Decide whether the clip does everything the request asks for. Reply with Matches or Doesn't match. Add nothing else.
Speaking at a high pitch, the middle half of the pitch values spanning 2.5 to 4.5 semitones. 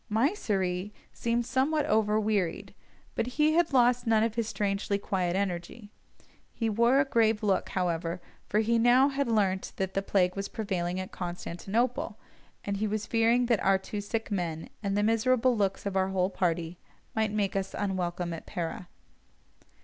Matches